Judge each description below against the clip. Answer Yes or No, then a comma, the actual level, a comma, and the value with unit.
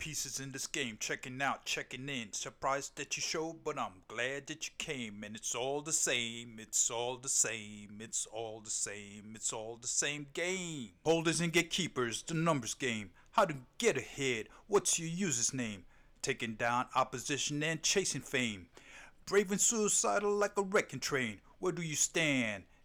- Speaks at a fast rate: No, average, 175 wpm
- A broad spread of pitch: Yes, wide, 6.0 semitones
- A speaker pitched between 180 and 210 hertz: No, low, 135 Hz